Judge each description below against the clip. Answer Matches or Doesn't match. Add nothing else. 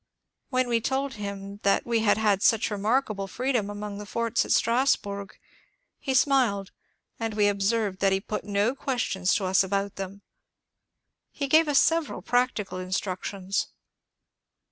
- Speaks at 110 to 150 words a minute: Matches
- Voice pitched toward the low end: Doesn't match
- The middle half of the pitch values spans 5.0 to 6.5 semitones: Doesn't match